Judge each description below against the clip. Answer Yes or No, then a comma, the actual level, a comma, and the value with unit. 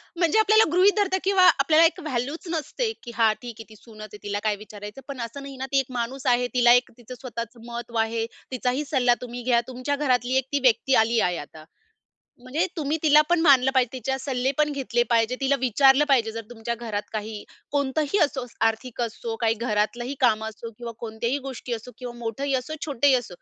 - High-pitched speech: Yes, very high, 250 Hz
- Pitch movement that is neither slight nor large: Yes, average, 3.3 semitones